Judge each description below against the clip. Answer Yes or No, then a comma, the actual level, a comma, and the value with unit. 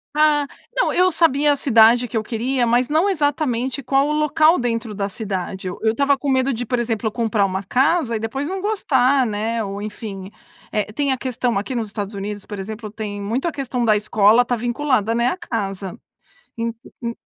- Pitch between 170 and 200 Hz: No, high, 235 Hz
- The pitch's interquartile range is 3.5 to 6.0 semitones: Yes, average, 4.3 semitones